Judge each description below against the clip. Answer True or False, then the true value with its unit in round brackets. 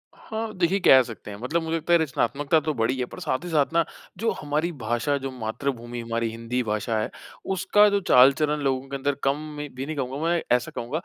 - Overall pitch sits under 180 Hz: True (140 Hz)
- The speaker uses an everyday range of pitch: True (4.9 semitones)